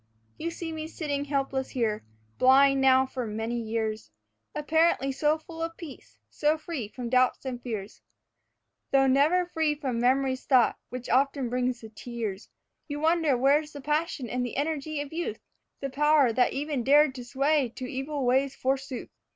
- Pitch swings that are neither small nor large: Yes, average, 3.2 semitones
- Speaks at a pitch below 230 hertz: No, very high, 270 Hz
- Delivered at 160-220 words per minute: Yes, average, 170 wpm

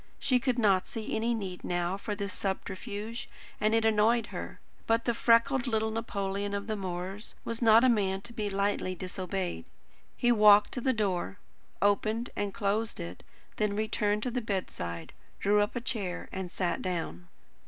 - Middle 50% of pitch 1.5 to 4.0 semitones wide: Yes, average, 2.9 semitones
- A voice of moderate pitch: No, high, 205 Hz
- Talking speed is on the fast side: No, average, 175 wpm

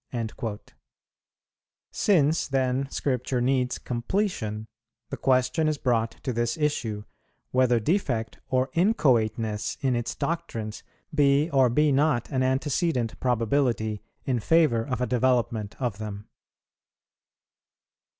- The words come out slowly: Yes, slow, 110 wpm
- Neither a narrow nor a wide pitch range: Yes, average, 3.8 semitones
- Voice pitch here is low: Yes, low, 125 Hz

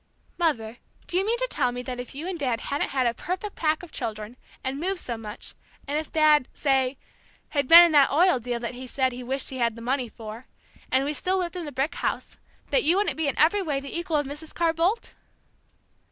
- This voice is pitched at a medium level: No, very high, 285 Hz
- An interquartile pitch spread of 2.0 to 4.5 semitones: No, average, 5.2 semitones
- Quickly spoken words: Yes, fast, 240 wpm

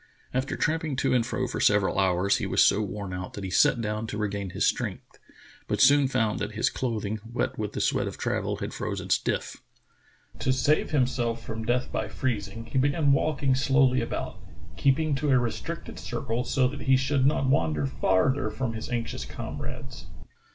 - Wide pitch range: No, average, 4.0 semitones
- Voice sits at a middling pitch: No, low, 120 Hz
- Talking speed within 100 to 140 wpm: No, average, 195 wpm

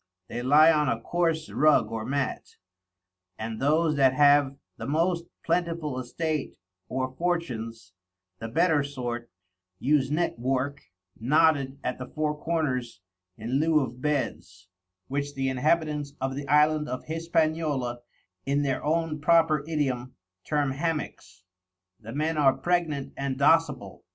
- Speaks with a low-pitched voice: No, medium, 145 Hz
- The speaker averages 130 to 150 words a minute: Yes, slow, 135 wpm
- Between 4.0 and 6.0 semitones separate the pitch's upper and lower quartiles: No, average, 3.5 semitones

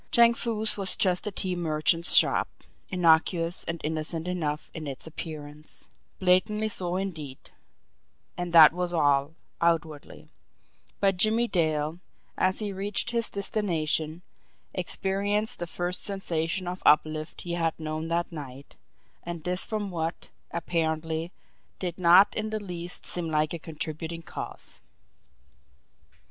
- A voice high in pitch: No, medium, 170 Hz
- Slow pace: Yes, slow, 130 wpm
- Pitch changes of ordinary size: Yes, average, 3.3 semitones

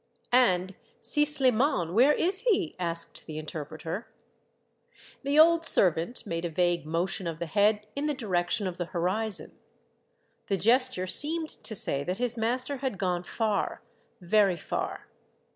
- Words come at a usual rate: Yes, average, 160 wpm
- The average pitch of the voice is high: Yes, high, 200 Hz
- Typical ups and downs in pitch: No, wide, 6.6 semitones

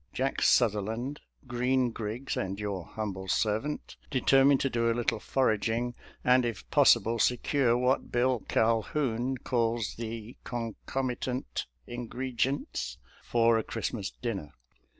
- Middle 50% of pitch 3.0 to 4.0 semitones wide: No, narrow, 2.5 semitones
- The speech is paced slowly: Yes, slow, 130 wpm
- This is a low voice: Yes, low, 120 Hz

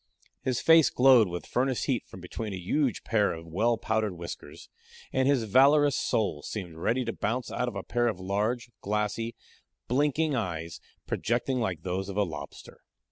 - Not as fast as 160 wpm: No, average, 175 wpm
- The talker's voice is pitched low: Yes, low, 110 Hz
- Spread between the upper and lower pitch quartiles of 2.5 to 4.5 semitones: No, average, 5.2 semitones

